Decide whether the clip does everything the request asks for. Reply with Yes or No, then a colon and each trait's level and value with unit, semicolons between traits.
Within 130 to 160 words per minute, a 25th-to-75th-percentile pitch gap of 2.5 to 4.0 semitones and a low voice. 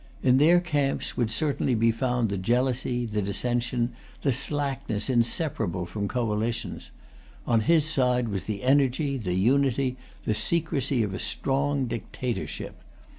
Yes: slow, 135 wpm; average, 3.5 semitones; low, 125 Hz